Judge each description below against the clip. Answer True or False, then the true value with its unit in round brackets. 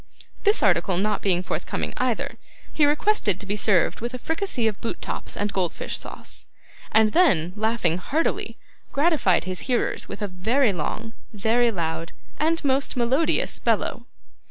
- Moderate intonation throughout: False (6.7 semitones)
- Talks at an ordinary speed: True (155 wpm)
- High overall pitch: True (220 Hz)